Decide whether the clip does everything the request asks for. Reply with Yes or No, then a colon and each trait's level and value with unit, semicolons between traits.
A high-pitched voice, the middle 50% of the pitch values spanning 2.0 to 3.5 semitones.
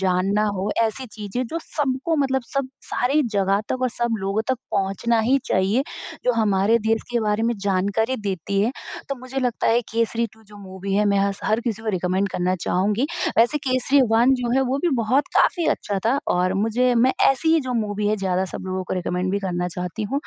No: high, 220 Hz; average, 4.3 semitones